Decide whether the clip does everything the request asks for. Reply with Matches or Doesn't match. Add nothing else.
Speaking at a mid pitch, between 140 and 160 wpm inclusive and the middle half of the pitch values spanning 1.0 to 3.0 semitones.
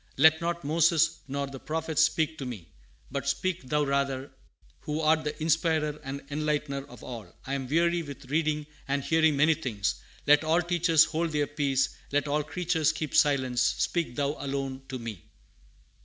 Doesn't match